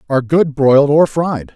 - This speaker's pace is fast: No, average, 195 wpm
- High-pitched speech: No, medium, 145 Hz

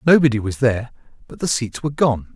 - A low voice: Yes, low, 125 Hz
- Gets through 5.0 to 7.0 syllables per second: Yes, 6.4 syllables/s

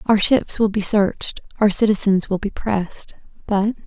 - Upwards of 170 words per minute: No, average, 155 wpm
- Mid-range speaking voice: No, high, 205 Hz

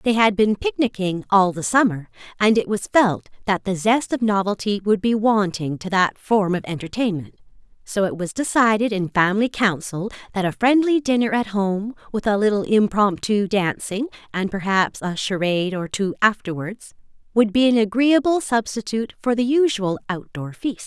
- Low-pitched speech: No, high, 210 Hz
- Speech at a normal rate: Yes, average, 170 wpm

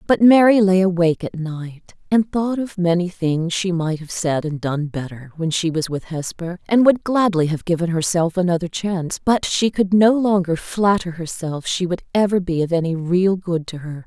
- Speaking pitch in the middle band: Yes, medium, 180 Hz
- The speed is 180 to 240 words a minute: Yes, fast, 205 wpm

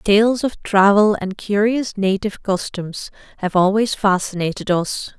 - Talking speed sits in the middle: No, slow, 125 wpm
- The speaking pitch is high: Yes, high, 200 Hz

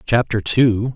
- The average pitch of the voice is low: Yes, low, 115 Hz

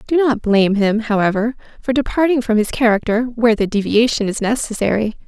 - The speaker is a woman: Yes, female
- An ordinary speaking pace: Yes, average, 170 wpm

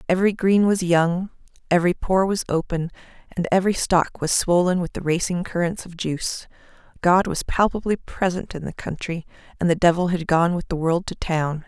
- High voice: No, medium, 175 Hz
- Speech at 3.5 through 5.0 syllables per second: No, 5.2 syllables/s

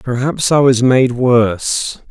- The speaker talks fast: No, average, 140 wpm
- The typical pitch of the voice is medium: No, low, 125 Hz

